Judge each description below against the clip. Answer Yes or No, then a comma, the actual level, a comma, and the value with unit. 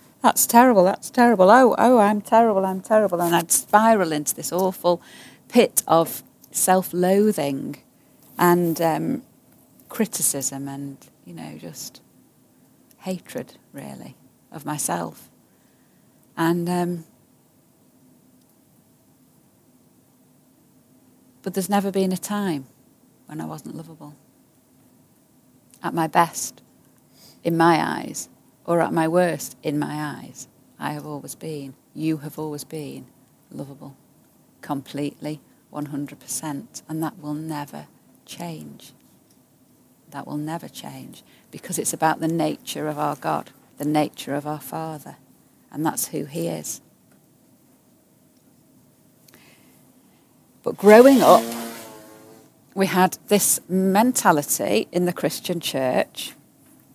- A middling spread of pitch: Yes, average, 4.1 semitones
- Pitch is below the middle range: No, medium, 160 Hz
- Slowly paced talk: Yes, slow, 110 wpm